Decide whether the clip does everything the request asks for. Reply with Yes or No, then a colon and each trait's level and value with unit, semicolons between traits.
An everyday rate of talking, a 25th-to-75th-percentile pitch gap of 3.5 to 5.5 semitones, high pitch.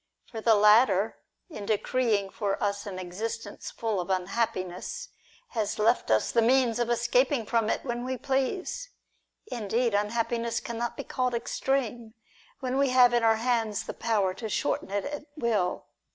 No: average, 160 wpm; average, 3.1 semitones; high, 230 Hz